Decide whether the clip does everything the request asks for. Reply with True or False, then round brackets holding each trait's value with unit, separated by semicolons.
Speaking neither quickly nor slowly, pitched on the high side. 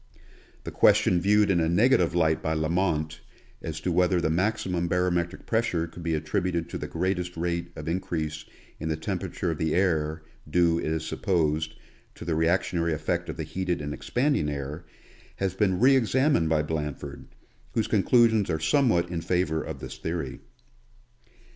False (165 wpm; 85 Hz)